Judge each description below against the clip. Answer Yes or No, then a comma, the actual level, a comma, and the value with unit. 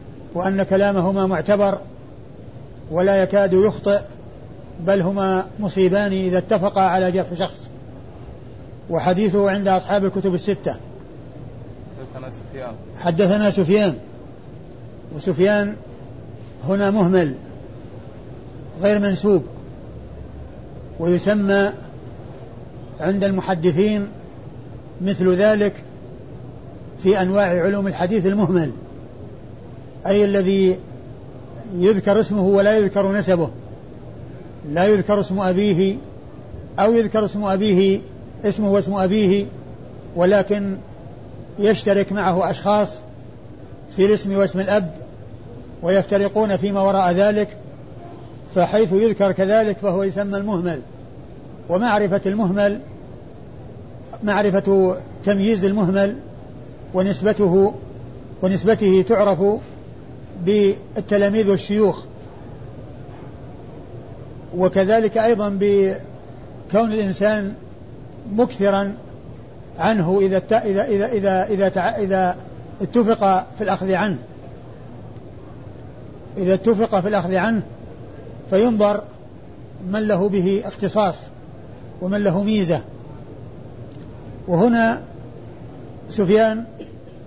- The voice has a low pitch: No, high, 190 Hz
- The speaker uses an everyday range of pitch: No, wide, 7.6 semitones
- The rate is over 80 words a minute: No, average, 75 wpm